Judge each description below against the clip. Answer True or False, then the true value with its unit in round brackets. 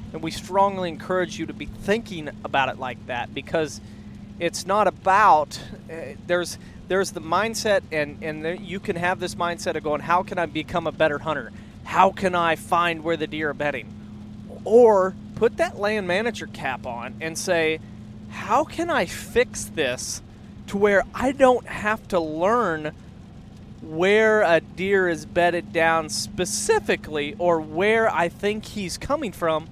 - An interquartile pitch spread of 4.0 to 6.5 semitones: True (4.6 semitones)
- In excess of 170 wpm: False (165 wpm)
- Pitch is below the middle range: False (175 Hz)